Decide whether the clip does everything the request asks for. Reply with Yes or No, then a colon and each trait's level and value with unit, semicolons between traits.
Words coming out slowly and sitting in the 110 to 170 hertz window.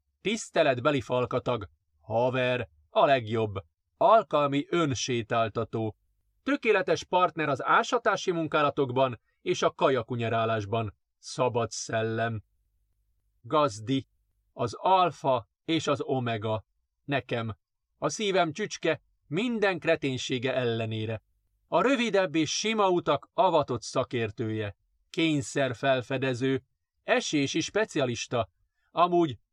Yes: slow, 85 wpm; low, 130 Hz